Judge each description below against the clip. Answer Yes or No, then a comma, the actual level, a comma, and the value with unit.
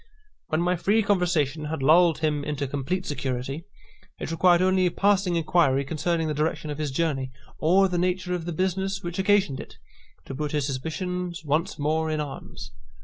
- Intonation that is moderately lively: Yes, average, 3.5 semitones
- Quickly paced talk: No, average, 180 wpm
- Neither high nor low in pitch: Yes, medium, 165 Hz